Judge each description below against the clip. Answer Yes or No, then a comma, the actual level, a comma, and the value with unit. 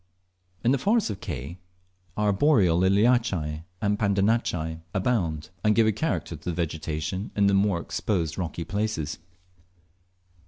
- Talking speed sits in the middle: No, slow, 130 wpm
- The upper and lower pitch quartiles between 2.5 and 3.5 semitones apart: No, average, 4.8 semitones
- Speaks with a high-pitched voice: No, very low, 95 Hz